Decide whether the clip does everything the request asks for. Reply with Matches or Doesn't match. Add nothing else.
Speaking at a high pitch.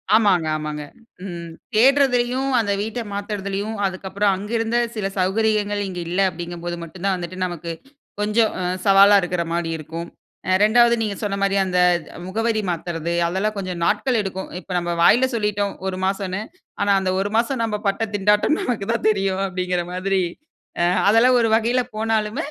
Matches